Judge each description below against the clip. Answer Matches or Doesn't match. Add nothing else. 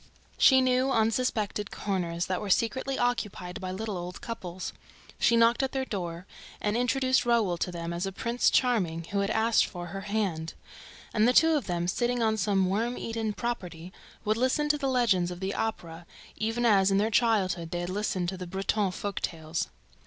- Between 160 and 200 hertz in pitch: Doesn't match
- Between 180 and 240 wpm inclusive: Matches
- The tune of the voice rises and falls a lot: Doesn't match